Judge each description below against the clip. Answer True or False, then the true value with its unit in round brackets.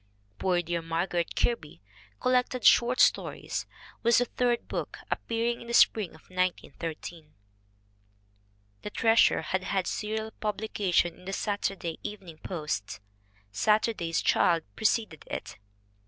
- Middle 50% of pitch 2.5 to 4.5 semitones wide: False (4.9 semitones)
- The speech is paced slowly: True (120 wpm)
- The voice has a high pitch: True (195 Hz)